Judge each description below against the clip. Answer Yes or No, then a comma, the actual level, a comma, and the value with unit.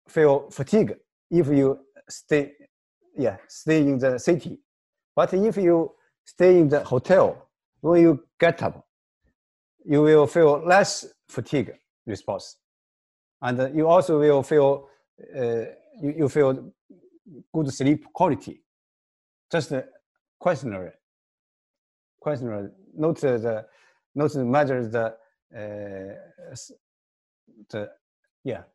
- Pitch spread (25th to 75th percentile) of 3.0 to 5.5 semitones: Yes, average, 5.0 semitones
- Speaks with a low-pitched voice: No, medium, 145 Hz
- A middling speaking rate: No, slow, 110 wpm